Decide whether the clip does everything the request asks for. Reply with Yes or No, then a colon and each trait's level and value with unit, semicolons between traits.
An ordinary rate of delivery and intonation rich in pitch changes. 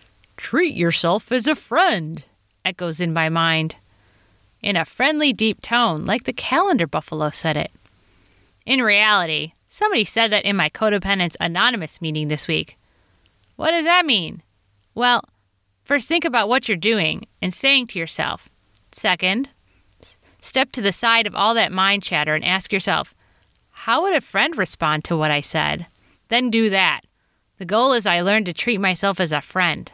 Yes: average, 165 wpm; wide, 6.7 semitones